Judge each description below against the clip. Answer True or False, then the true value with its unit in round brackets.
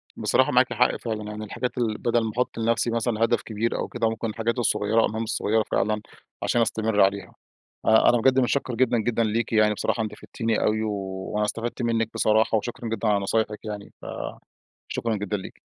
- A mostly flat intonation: True (1.6 semitones)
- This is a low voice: True (110 Hz)